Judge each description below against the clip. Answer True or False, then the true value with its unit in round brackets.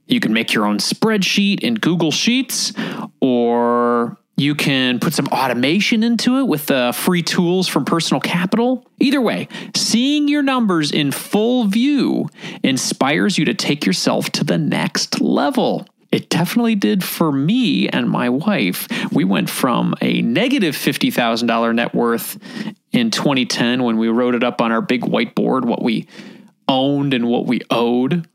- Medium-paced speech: True (160 wpm)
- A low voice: False (185 Hz)